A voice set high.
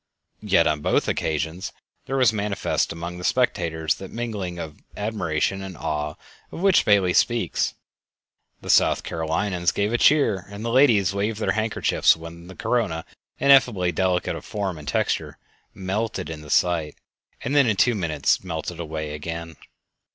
No: very low, 95 Hz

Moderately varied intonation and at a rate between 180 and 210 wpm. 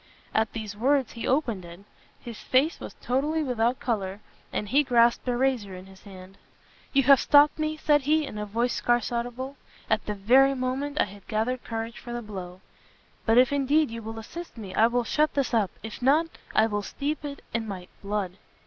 Yes: average, 4.6 semitones; fast, 205 wpm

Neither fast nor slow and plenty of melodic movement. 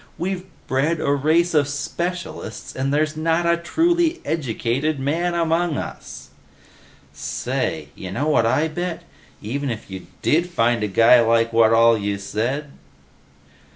Yes: average, 150 wpm; wide, 6.6 semitones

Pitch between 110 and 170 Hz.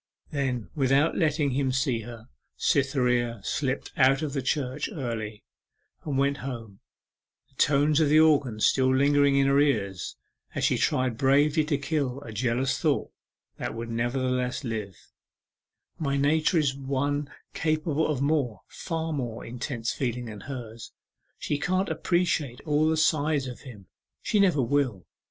Yes: low, 135 Hz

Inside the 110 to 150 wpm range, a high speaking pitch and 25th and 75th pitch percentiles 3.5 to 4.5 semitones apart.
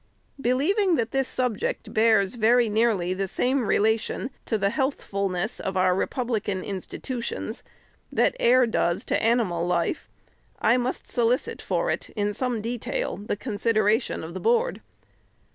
Yes: average, 145 wpm; high, 225 Hz; average, 4.2 semitones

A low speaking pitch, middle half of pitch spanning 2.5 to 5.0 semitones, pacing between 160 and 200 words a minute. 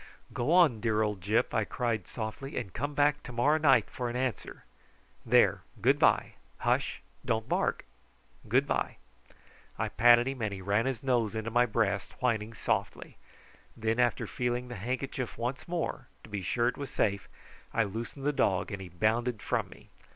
Yes: low, 120 Hz; average, 2.9 semitones; average, 180 wpm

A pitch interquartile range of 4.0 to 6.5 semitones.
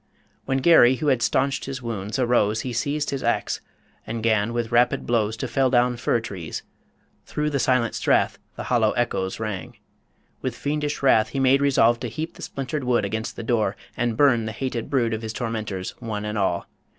No: average, 3.2 semitones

